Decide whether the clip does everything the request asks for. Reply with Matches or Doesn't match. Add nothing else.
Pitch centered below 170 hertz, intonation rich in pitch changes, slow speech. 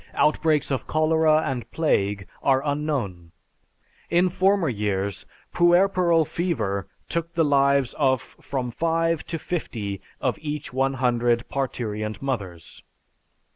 Matches